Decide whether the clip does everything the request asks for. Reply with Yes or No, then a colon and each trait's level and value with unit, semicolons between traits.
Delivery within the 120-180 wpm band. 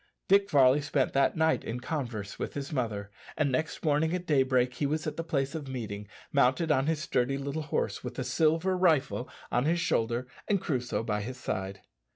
No: average, 195 wpm